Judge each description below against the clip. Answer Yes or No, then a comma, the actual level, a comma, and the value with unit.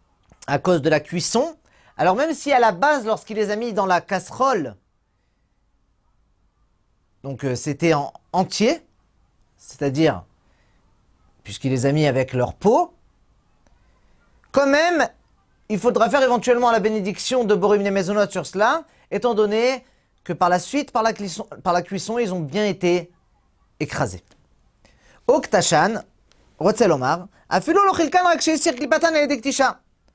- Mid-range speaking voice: No, high, 205 Hz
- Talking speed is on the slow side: Yes, slow, 125 wpm